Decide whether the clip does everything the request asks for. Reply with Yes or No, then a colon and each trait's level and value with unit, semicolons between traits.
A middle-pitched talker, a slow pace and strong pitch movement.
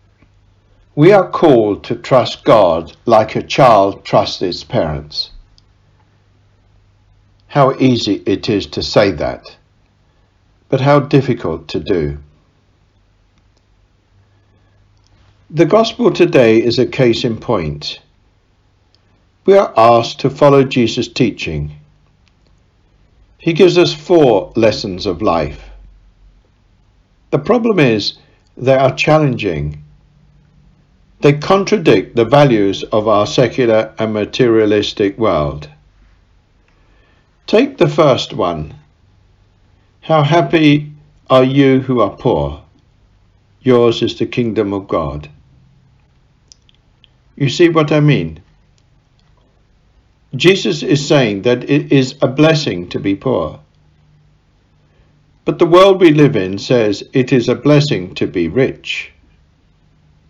No: low, 105 Hz; slow, 110 wpm; wide, 6.4 semitones